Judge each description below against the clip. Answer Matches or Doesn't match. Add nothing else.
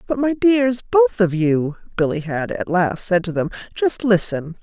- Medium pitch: Doesn't match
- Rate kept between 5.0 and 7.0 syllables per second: Doesn't match